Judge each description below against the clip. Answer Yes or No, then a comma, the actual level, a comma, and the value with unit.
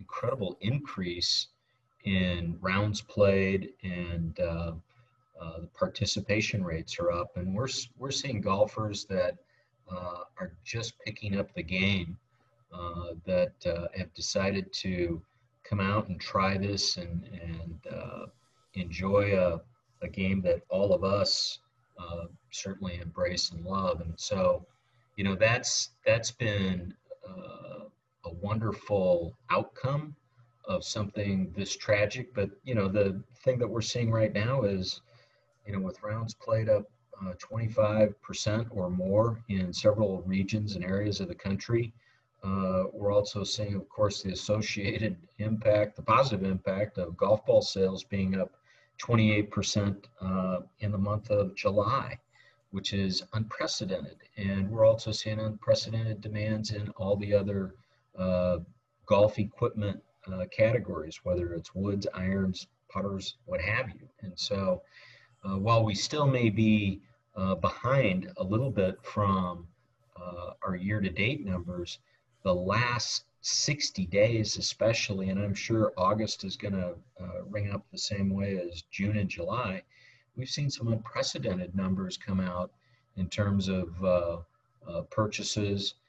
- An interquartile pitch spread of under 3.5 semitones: Yes, average, 2.8 semitones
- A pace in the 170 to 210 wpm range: No, average, 145 wpm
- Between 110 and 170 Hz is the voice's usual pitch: No, low, 100 Hz